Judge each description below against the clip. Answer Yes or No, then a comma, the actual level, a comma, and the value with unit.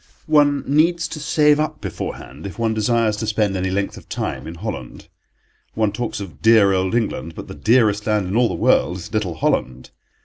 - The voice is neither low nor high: No, low, 110 Hz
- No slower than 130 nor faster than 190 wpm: No, average, 200 wpm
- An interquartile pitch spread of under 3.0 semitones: No, average, 4.4 semitones